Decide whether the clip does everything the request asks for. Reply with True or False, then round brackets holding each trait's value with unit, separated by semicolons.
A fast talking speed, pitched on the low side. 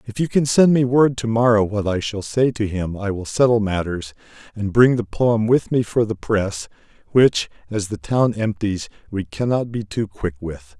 True (210 wpm; 110 Hz)